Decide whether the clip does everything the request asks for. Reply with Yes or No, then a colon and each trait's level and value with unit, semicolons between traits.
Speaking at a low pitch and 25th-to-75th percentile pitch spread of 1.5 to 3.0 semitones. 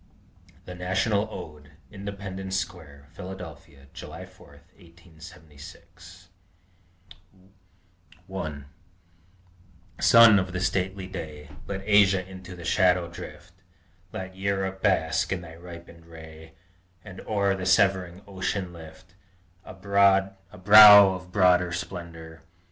Yes: very low, 90 Hz; narrow, 2.4 semitones